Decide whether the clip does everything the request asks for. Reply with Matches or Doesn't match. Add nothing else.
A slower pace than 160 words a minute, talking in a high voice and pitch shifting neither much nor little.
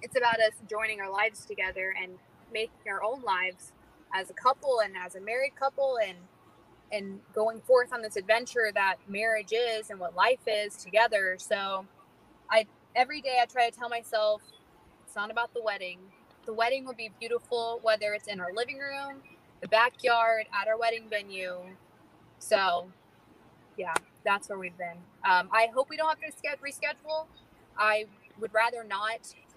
Doesn't match